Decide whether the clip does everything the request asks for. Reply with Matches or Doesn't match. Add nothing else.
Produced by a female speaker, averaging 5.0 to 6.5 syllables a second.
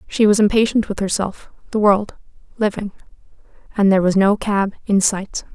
Matches